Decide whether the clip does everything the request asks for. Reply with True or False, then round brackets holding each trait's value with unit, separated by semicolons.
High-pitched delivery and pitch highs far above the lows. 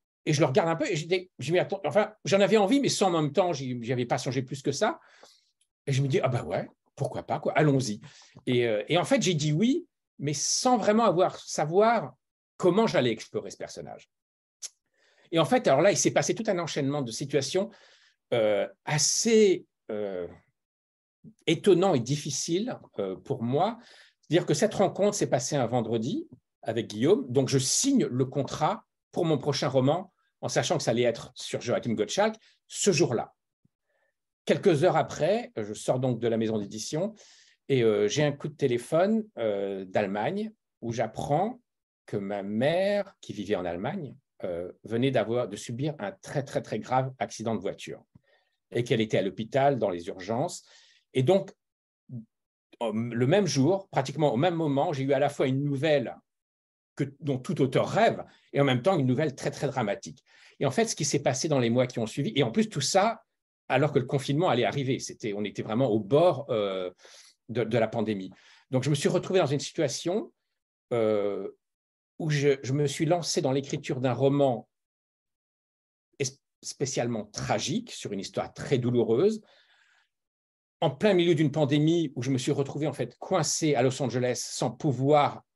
False (140 Hz; 6.5 semitones)